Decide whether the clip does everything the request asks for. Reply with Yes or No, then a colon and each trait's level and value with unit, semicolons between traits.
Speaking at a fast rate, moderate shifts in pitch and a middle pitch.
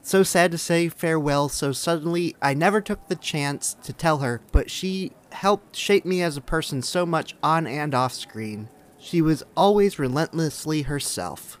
No: average, 175 wpm; average, 3.8 semitones; medium, 160 Hz